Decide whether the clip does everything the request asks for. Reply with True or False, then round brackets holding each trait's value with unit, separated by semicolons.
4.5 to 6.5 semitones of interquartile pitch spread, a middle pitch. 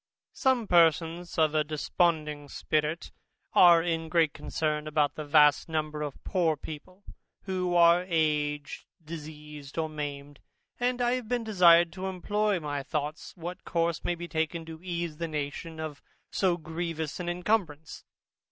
False (2.6 semitones; 160 Hz)